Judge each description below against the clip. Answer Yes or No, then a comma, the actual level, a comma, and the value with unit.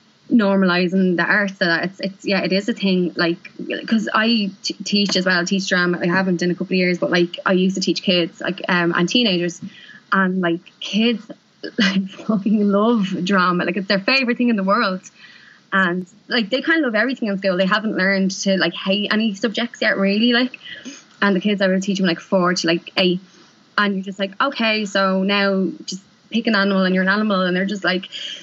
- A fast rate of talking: Yes, fast, 225 wpm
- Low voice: No, high, 195 Hz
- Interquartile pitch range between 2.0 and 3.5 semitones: Yes, narrow, 2.5 semitones